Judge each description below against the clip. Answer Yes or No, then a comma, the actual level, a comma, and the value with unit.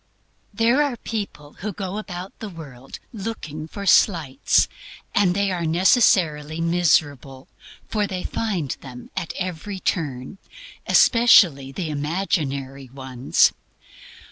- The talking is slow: Yes, slow, 115 wpm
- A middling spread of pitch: No, wide, 5.8 semitones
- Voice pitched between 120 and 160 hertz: No, medium, 170 Hz